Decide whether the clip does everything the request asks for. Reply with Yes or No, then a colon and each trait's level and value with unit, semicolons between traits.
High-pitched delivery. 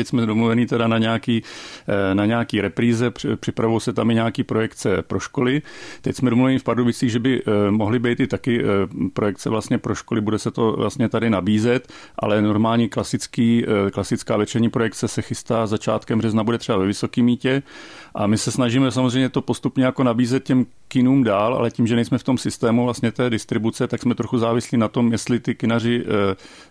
No: low, 115 Hz